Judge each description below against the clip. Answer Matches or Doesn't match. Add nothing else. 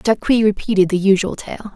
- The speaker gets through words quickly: Doesn't match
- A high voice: Matches